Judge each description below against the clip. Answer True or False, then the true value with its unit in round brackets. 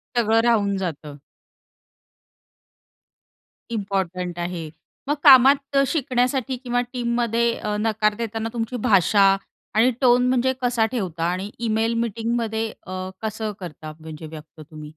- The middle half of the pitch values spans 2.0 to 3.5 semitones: False (4.5 semitones)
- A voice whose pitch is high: True (220 Hz)